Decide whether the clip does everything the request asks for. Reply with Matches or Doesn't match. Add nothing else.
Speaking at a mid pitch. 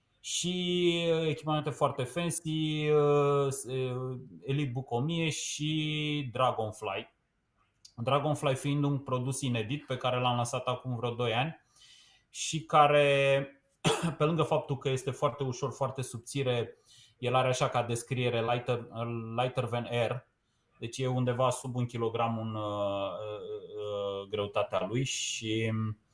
Doesn't match